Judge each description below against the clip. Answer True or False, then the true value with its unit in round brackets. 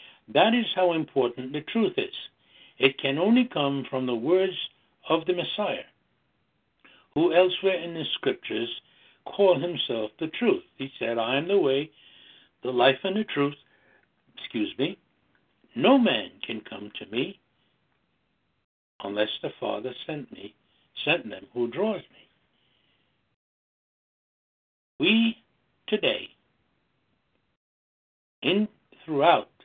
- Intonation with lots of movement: True (7.0 semitones)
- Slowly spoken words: True (120 wpm)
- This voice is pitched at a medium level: True (170 Hz)